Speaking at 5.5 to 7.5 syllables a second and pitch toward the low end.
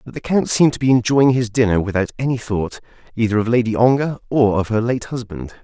Yes: 6.0 syllables/s; low, 115 Hz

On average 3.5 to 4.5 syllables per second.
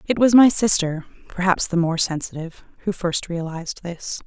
No: 5.2 syllables/s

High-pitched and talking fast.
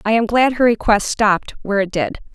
Yes: high, 215 Hz; fast, 230 wpm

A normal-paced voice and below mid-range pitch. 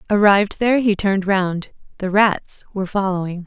No: average, 155 wpm; high, 195 Hz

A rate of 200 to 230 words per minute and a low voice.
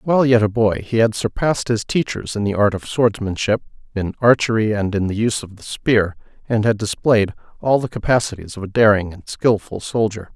Yes: fast, 205 wpm; low, 110 Hz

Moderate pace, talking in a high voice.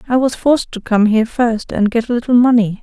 No: fast, 255 wpm; high, 235 Hz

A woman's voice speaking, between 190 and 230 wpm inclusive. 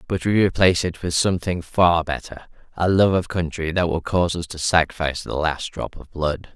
No: male; average, 200 wpm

